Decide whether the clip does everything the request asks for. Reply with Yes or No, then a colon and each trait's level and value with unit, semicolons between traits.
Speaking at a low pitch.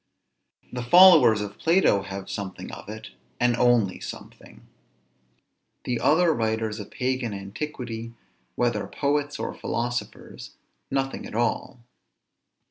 Yes: low, 120 Hz